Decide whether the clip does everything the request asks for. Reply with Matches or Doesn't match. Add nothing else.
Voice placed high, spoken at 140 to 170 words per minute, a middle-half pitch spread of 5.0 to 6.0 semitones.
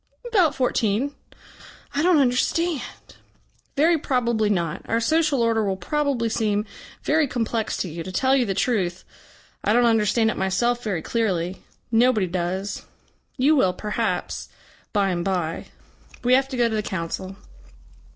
Matches